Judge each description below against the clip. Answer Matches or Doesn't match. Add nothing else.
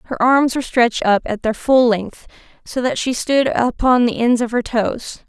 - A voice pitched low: Doesn't match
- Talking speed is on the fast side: Matches